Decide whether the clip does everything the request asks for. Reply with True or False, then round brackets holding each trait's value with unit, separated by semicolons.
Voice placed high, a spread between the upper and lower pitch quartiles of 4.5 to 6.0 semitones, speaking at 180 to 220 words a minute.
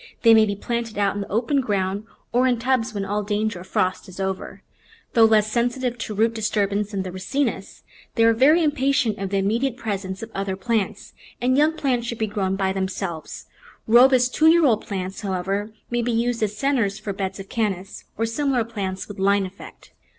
False (215 Hz; 3.5 semitones; 200 wpm)